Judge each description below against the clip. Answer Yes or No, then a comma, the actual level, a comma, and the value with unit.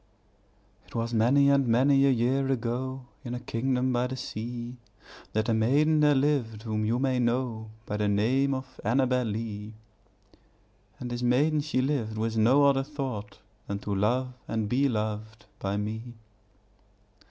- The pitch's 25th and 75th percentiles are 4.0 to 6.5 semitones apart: No, average, 3.2 semitones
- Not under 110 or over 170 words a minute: Yes, average, 160 wpm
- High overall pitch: No, low, 120 Hz